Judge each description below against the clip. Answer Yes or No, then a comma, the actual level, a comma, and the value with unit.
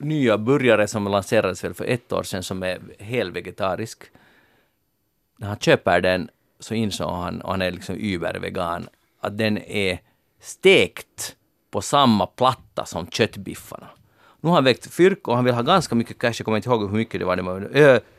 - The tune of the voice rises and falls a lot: No, average, 4.5 semitones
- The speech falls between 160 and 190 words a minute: Yes, average, 185 wpm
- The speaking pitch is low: Yes, low, 110 Hz